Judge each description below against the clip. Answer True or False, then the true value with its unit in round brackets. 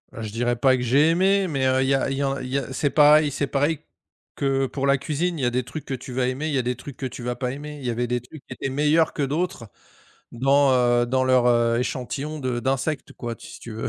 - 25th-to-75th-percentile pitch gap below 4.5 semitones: True (2.9 semitones)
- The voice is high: False (135 Hz)